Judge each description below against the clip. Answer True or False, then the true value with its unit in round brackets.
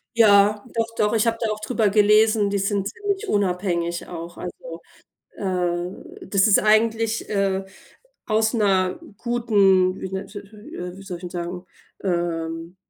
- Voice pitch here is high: True (200 Hz)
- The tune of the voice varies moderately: True (3.1 semitones)